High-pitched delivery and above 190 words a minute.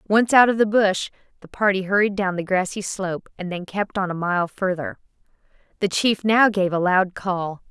Yes: high, 195 Hz; fast, 205 wpm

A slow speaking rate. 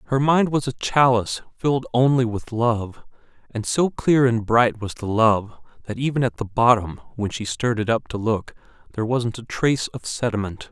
No: average, 195 wpm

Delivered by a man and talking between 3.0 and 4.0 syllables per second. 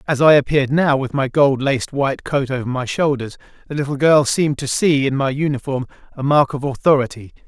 No: male; 5.9 syllables/s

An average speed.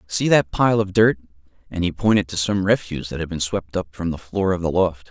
No: fast, 260 wpm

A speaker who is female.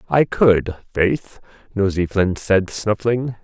No: male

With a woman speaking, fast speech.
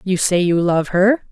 Yes: female; fast, 230 wpm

